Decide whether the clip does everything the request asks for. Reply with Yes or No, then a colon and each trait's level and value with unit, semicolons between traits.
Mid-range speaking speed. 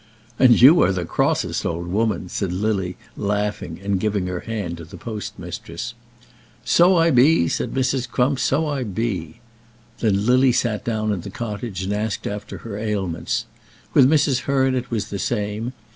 Yes: average, 170 wpm